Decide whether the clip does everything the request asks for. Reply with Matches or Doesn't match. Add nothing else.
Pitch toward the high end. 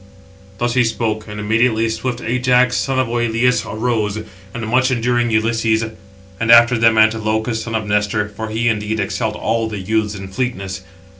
Doesn't match